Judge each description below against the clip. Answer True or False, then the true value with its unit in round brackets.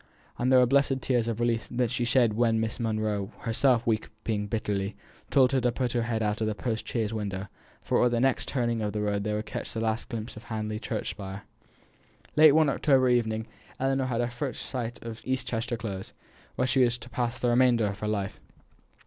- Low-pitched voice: True (115 Hz)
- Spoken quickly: True (215 wpm)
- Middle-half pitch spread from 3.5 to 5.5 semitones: False (2.5 semitones)